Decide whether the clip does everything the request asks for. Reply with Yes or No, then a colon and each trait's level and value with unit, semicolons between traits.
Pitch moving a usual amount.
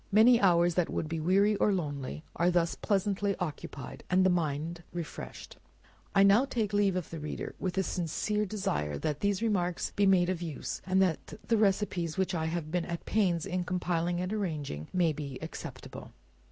Yes: average, 3.3 semitones